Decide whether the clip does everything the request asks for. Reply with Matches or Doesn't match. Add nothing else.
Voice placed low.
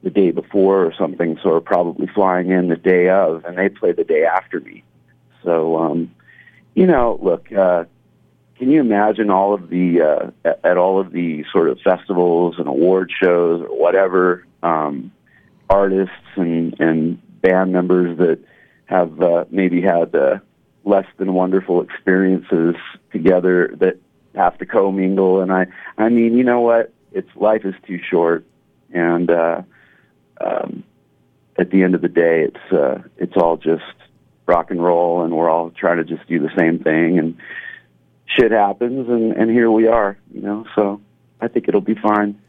Matches